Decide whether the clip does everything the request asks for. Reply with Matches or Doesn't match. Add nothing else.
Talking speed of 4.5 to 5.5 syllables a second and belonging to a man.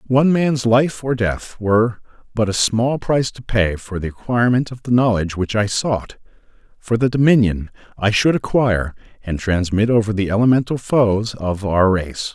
Matches